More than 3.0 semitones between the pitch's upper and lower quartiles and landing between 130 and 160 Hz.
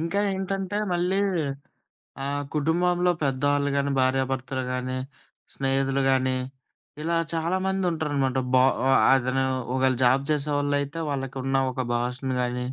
Yes: average, 3.8 semitones; medium, 140 Hz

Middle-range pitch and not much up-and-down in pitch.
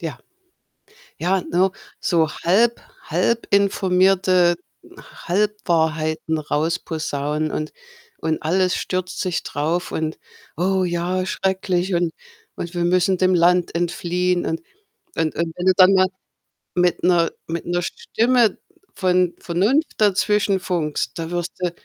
Yes: medium, 180 Hz; narrow, 2.0 semitones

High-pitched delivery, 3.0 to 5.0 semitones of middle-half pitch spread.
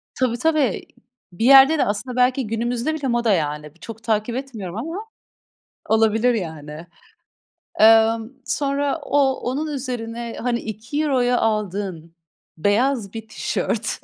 Yes: high, 235 Hz; average, 4.0 semitones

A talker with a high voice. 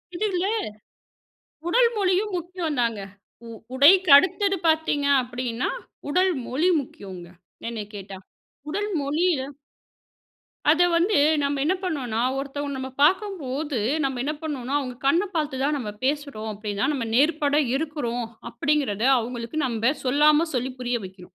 Yes: very high, 285 Hz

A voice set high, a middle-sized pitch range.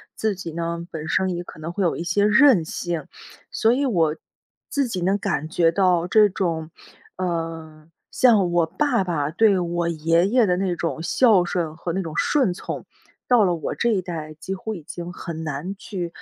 No: medium, 175 Hz; average, 3.4 semitones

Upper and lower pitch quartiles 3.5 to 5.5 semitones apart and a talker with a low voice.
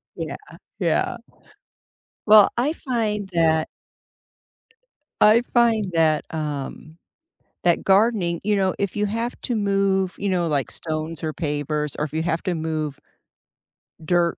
No: average, 4.8 semitones; medium, 175 Hz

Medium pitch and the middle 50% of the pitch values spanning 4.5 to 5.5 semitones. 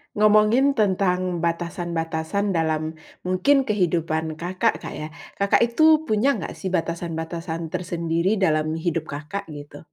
No: medium, 175 Hz; average, 3.9 semitones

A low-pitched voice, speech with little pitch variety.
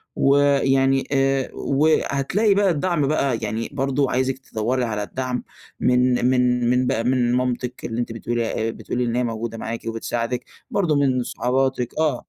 Yes: low, 125 Hz; narrow, 2.3 semitones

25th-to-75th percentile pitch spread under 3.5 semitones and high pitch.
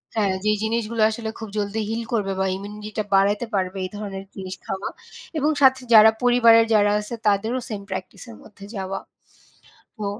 Yes: narrow, 2.4 semitones; high, 210 Hz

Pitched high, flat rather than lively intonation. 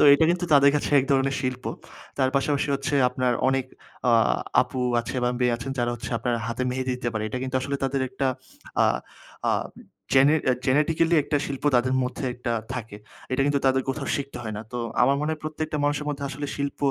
No: low, 135 Hz; narrow, 2.1 semitones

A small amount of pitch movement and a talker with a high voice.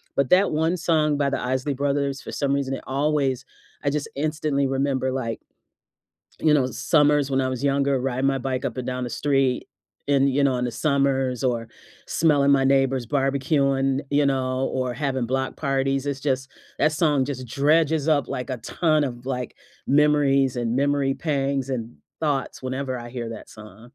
No: narrow, 1.7 semitones; low, 135 Hz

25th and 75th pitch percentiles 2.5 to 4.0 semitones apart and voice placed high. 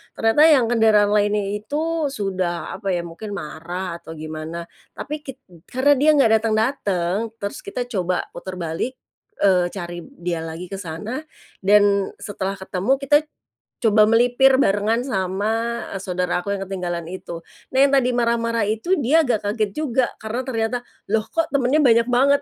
No: average, 4.7 semitones; high, 210 Hz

